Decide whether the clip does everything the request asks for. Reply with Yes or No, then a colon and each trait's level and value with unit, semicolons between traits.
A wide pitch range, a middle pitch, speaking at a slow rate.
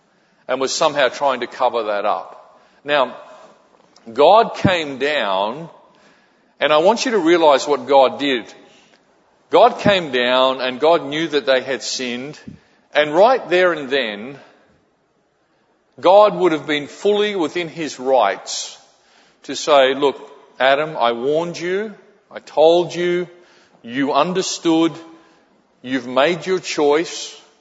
No: average, 4.4 semitones; medium, 155 Hz; slow, 130 wpm